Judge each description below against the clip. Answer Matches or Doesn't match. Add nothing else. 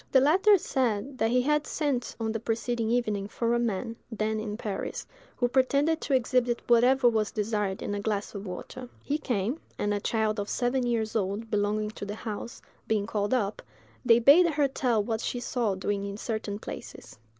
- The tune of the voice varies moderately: Matches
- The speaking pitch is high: Matches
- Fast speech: Doesn't match